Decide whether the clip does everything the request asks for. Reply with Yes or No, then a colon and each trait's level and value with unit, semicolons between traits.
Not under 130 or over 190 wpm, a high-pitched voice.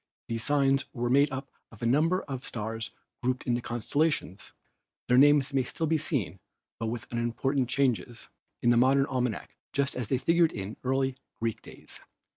No: average, 170 wpm; low, 130 Hz